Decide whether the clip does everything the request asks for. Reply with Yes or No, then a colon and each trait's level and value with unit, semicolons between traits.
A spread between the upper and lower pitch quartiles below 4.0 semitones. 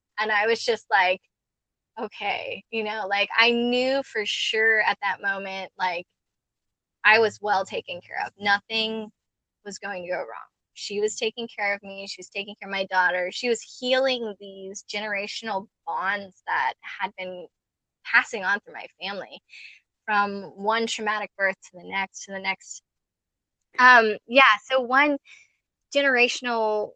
Yes: average, 3.3 semitones